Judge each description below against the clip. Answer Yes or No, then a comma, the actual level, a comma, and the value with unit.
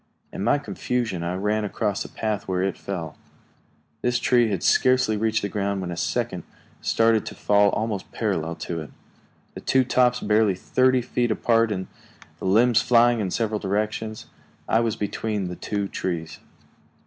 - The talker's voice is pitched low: Yes, low, 105 Hz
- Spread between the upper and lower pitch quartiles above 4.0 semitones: No, average, 3.1 semitones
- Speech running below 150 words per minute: No, average, 170 wpm